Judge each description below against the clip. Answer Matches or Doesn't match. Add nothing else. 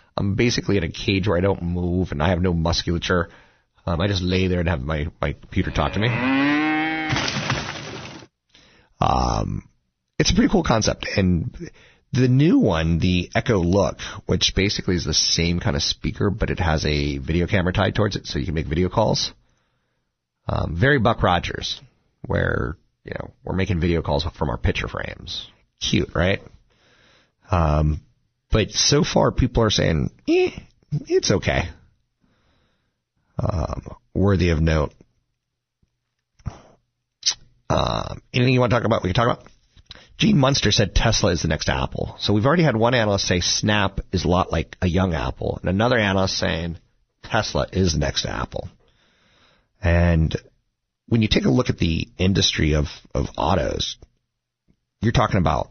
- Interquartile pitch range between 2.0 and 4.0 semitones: Doesn't match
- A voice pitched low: Matches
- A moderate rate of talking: Matches